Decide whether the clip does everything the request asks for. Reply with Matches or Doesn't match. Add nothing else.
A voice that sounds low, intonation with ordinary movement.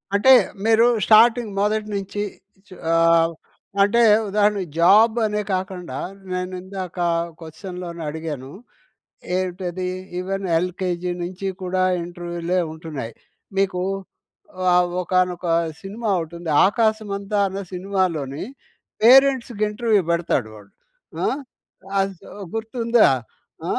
Doesn't match